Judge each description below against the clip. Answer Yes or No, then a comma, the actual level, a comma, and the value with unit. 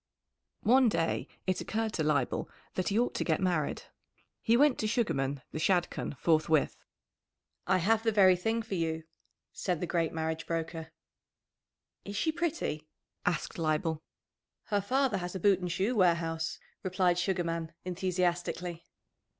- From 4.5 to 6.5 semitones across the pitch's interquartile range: No, average, 3.9 semitones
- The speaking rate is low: No, average, 150 wpm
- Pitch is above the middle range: No, medium, 180 Hz